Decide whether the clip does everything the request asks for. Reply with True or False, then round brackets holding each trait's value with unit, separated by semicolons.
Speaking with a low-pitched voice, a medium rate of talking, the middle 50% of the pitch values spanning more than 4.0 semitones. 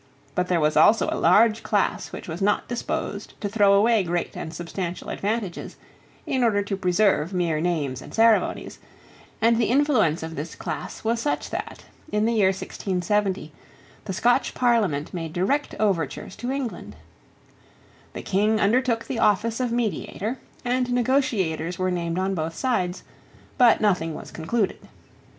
False (205 Hz; 155 wpm; 4.8 semitones)